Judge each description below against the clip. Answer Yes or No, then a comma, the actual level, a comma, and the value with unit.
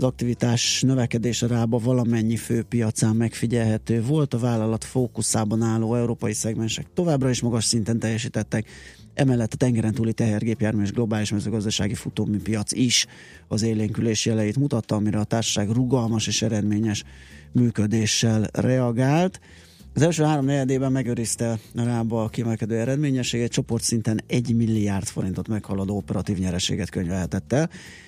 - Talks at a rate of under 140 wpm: Yes, average, 130 wpm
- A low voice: Yes, low, 115 Hz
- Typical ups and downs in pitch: No, narrow, 2.2 semitones